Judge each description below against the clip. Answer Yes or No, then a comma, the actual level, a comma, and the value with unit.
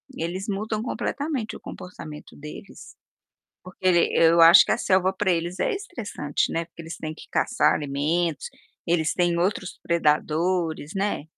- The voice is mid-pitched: Yes, medium, 175 Hz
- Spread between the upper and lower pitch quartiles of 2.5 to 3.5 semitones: Yes, average, 3.2 semitones